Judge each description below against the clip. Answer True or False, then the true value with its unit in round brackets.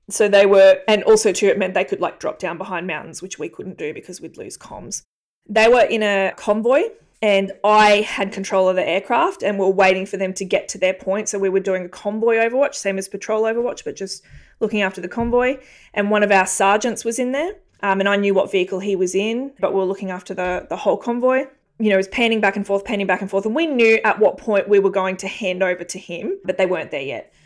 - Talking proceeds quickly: True (260 wpm)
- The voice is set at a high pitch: True (200 Hz)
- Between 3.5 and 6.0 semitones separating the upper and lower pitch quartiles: False (2.7 semitones)